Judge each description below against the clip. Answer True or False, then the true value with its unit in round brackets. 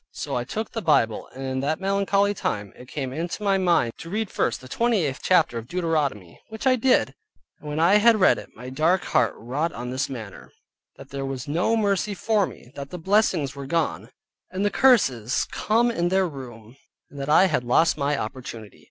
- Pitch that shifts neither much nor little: False (7.2 semitones)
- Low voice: False (155 Hz)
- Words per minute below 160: False (205 wpm)